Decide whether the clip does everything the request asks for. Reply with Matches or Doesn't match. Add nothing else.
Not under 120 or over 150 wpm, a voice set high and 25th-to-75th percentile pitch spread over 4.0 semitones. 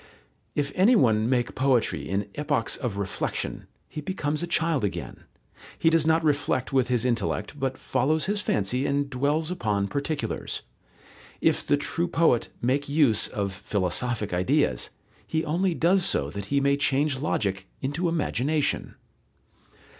Doesn't match